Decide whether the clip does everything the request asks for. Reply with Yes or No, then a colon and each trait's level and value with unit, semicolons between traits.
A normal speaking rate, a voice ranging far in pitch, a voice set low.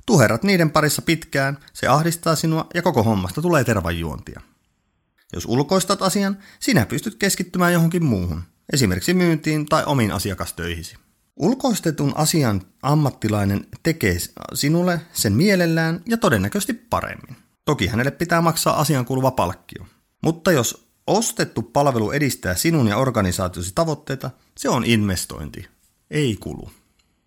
No: average, 125 wpm; wide, 7.7 semitones; medium, 145 Hz